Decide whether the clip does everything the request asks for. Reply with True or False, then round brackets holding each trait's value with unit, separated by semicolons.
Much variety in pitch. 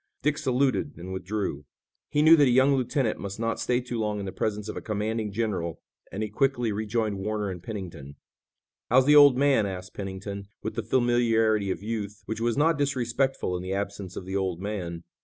False (4.0 semitones)